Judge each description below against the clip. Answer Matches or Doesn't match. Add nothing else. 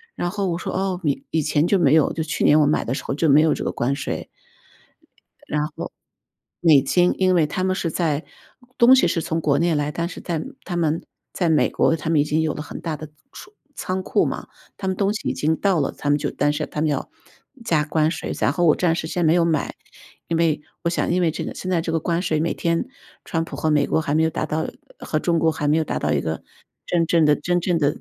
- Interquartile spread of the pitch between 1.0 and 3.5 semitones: Matches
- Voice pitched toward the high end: Doesn't match